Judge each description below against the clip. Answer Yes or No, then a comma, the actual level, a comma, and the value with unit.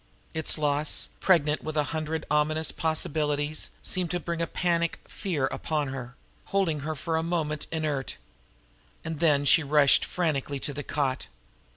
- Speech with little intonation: Yes, narrow, 2.0 semitones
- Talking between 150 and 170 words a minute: Yes, average, 155 wpm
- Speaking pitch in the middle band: Yes, medium, 155 Hz